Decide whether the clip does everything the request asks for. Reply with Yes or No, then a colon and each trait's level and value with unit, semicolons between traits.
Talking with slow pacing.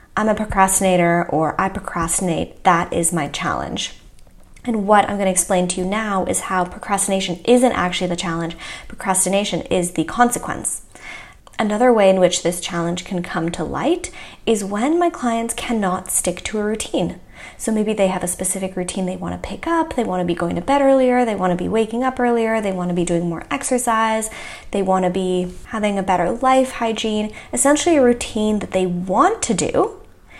No: average, 195 wpm